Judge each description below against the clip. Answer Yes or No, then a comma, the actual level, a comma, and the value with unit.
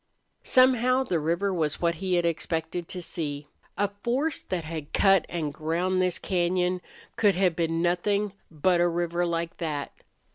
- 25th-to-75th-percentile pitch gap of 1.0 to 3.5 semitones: Yes, narrow, 2.4 semitones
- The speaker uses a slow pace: No, average, 160 wpm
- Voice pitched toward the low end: No, medium, 175 Hz